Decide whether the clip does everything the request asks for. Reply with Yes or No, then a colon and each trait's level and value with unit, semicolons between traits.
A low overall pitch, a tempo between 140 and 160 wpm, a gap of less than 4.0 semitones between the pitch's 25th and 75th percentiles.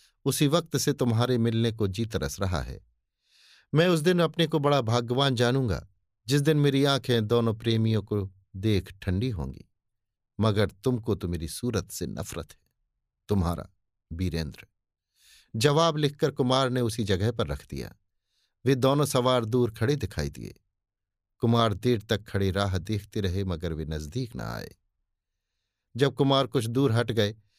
No: low, 110 Hz; average, 155 wpm; average, 5.1 semitones